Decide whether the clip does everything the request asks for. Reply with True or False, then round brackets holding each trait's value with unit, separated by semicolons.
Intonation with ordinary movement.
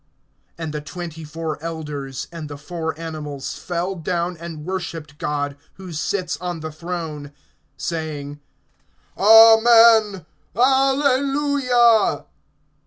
False (6.0 semitones)